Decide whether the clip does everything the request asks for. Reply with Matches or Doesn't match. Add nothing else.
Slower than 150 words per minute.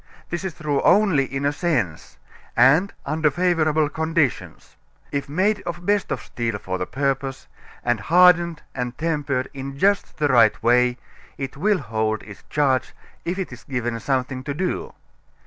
Doesn't match